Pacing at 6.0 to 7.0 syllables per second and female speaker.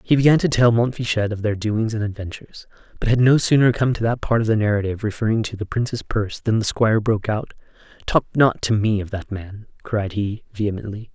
No: 6.1 syllables/s; male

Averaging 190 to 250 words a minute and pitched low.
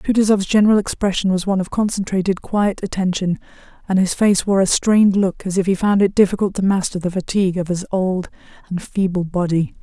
No: average, 195 wpm; high, 190 Hz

